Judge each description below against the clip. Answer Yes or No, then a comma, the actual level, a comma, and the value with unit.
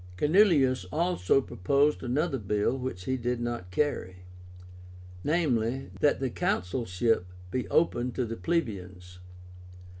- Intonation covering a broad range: Yes, wide, 6.3 semitones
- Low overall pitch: Yes, low, 125 Hz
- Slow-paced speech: Yes, slow, 115 wpm